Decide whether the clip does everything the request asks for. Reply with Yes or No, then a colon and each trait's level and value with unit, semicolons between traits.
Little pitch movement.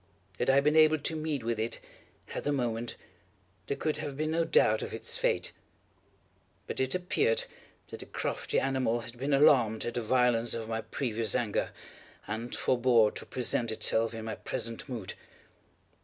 No: average, 3.7 semitones